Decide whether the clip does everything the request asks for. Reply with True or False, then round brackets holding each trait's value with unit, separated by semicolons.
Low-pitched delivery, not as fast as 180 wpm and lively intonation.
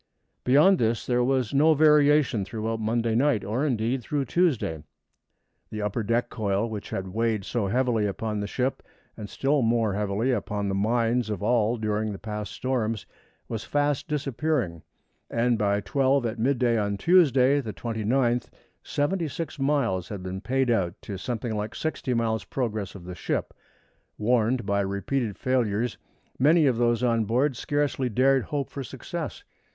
False (115 Hz; 160 wpm; 4.1 semitones)